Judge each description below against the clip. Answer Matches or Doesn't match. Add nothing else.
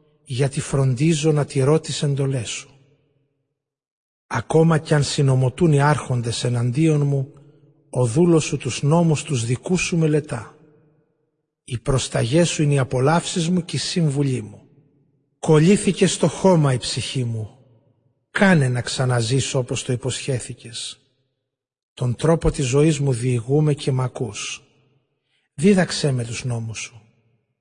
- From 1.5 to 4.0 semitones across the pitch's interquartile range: Matches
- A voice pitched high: Doesn't match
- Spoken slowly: Doesn't match